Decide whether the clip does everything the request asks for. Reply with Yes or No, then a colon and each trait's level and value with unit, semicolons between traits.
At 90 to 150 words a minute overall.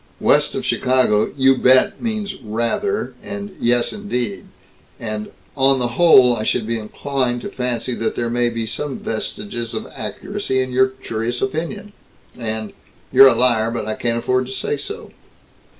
No: average, 165 wpm